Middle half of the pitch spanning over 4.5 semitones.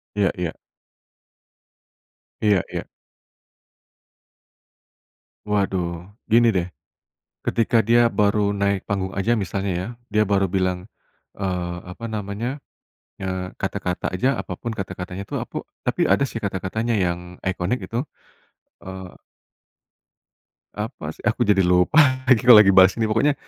No: average, 3.3 semitones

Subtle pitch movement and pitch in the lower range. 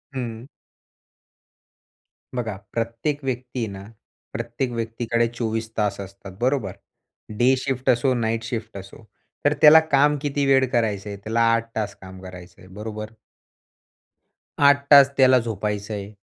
No: average, 3.3 semitones; low, 115 Hz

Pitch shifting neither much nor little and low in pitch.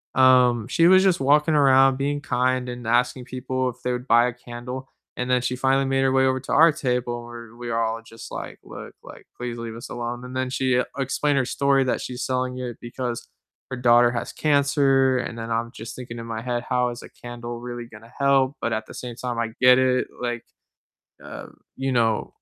No: narrow, 1.8 semitones; low, 125 Hz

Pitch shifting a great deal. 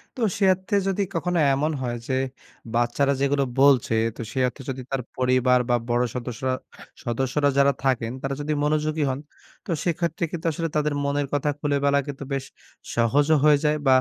No: average, 2.9 semitones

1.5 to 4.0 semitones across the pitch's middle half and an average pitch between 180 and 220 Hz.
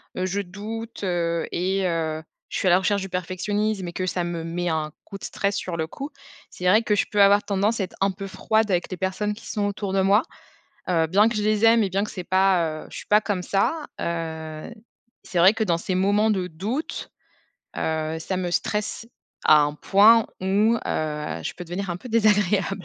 Yes: average, 3.2 semitones; high, 190 Hz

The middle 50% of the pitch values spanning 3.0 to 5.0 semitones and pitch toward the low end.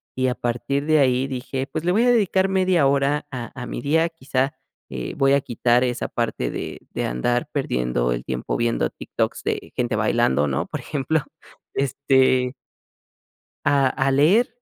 Yes: average, 3.4 semitones; low, 130 Hz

